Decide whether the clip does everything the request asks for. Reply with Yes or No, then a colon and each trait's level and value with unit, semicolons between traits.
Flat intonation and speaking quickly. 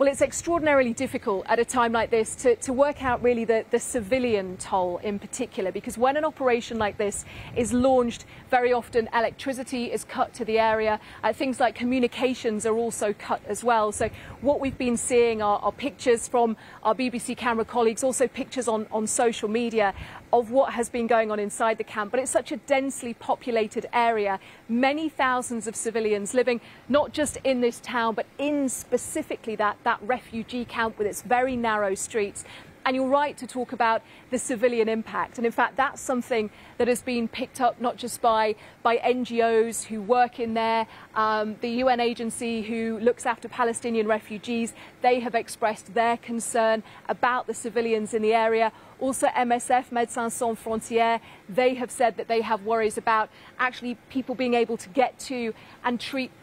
No: narrow, 2.1 semitones; average, 185 wpm